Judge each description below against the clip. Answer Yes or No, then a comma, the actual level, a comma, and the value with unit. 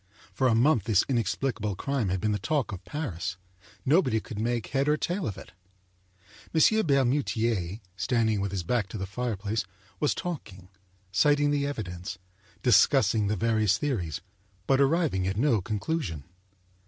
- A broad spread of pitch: Yes, wide, 6.1 semitones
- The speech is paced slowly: No, average, 155 wpm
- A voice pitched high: No, low, 115 Hz